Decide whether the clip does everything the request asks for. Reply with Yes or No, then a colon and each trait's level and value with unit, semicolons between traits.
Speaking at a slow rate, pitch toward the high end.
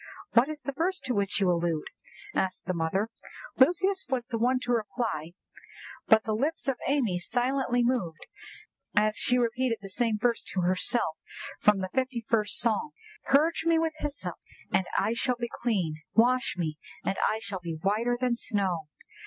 No: average, 170 wpm; high, 235 Hz